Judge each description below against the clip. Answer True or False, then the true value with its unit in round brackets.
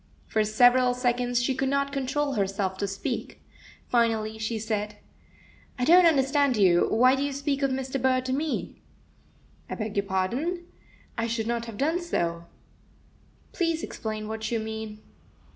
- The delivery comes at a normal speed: True (155 wpm)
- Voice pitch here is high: True (245 Hz)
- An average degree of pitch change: True (4.0 semitones)